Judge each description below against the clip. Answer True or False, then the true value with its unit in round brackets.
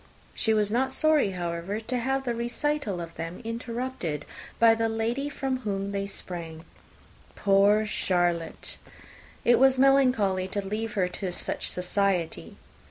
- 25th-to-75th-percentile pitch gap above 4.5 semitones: True (5.2 semitones)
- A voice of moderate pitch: False (210 Hz)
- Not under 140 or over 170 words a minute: True (155 wpm)